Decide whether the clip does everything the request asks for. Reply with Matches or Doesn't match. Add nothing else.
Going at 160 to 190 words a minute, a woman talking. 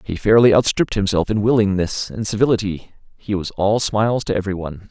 Doesn't match